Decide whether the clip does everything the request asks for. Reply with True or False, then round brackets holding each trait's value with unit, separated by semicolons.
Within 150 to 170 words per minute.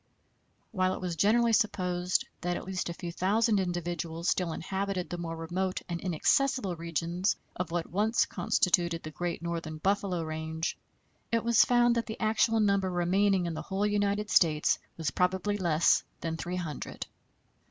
True (165 wpm)